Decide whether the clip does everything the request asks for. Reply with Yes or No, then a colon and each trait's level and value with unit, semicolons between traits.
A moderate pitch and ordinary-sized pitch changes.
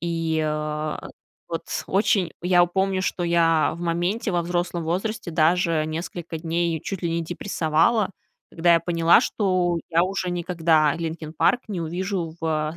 No: medium, 170 Hz; narrow, 1.8 semitones